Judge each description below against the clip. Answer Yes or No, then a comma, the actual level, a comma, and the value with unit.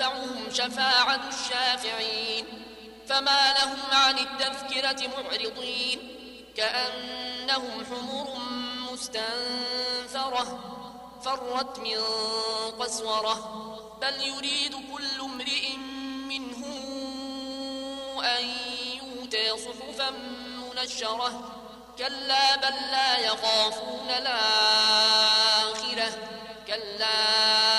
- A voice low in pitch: No, very high, 250 Hz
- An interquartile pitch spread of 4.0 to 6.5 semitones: No, average, 3.1 semitones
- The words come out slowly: Yes, slow, 60 wpm